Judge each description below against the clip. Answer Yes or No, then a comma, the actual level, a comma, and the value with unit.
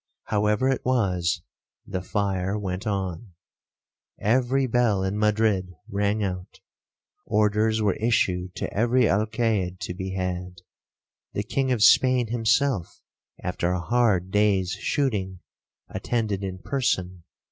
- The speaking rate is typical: No, slow, 115 wpm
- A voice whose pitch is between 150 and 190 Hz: No, low, 105 Hz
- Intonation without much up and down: No, average, 3.7 semitones